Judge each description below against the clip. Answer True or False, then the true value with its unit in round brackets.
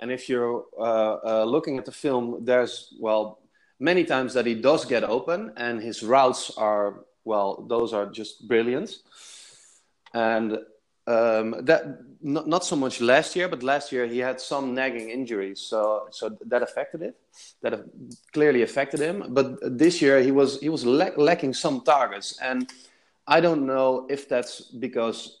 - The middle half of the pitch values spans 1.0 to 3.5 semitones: True (3.2 semitones)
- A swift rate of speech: False (170 wpm)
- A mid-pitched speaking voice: False (125 Hz)